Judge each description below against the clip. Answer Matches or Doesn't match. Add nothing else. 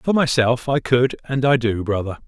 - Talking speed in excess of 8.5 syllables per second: Doesn't match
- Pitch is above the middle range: Doesn't match